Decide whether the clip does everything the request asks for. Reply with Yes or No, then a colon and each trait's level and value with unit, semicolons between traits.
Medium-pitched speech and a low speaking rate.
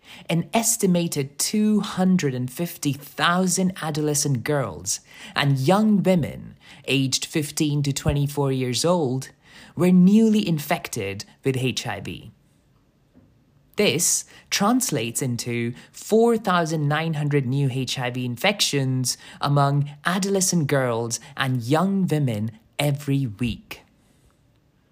Yes: medium, 145 Hz; slow, 80 wpm